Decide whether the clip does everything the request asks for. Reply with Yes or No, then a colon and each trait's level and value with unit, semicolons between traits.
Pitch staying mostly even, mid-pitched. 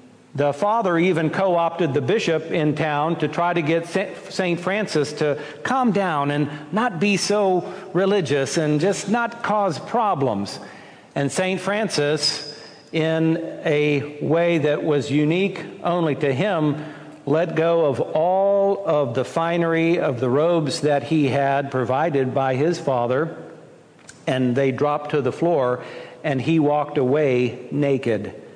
No: average, 3.9 semitones; medium, 155 Hz